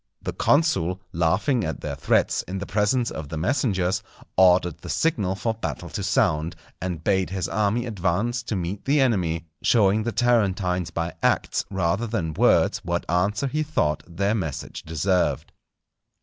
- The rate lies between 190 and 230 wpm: No, average, 160 wpm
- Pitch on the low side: Yes, very low, 95 Hz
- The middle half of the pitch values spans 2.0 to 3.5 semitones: No, average, 4.7 semitones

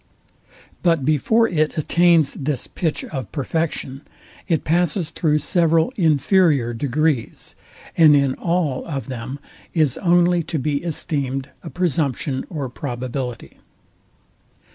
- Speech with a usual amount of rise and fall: Yes, average, 3.8 semitones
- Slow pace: Yes, slow, 115 wpm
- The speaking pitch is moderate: Yes, medium, 150 Hz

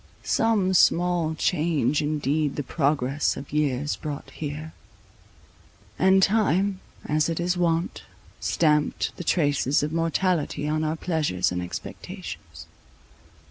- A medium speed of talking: No, slow, 115 wpm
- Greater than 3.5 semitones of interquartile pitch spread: No, average, 3.2 semitones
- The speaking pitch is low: No, medium, 155 Hz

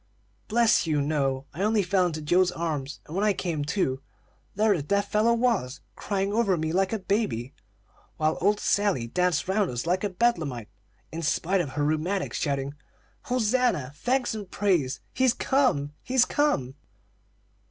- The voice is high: No, medium, 180 Hz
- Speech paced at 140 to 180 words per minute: Yes, average, 165 wpm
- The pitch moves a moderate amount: No, wide, 6.2 semitones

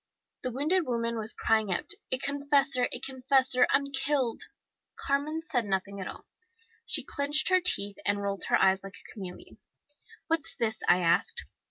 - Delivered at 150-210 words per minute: Yes, average, 165 wpm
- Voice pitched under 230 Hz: No, very high, 255 Hz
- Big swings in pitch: Yes, wide, 5.8 semitones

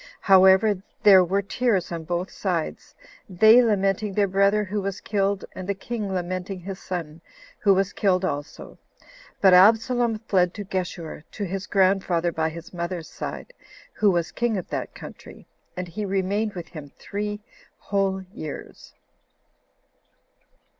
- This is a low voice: No, high, 190 Hz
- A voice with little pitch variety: Yes, narrow, 2.3 semitones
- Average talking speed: Yes, average, 145 wpm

